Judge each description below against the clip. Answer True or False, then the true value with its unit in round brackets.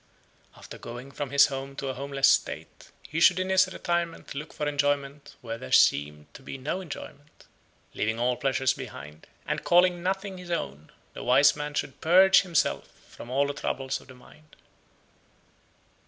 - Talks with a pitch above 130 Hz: True (140 Hz)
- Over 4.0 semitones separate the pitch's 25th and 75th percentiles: True (4.7 semitones)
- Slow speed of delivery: False (170 wpm)